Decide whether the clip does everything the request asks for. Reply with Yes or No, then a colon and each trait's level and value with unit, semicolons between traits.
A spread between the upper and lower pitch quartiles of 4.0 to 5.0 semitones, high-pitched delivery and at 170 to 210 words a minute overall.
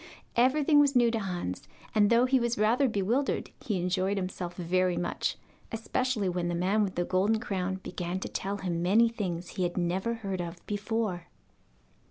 Yes: average, 4.3 semitones; high, 195 Hz; average, 180 wpm